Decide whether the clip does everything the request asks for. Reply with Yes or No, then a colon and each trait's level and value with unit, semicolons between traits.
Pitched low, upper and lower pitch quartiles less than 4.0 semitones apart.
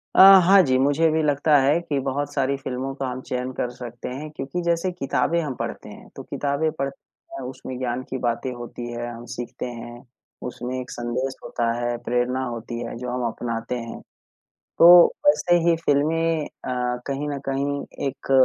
Yes: low, 130 Hz; average, 2.9 semitones